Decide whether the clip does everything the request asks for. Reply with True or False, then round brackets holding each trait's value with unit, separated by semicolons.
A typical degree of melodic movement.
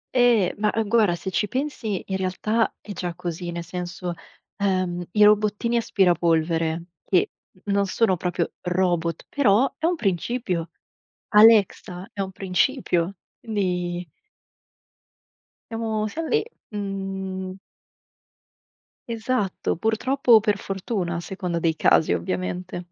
True (3.8 semitones)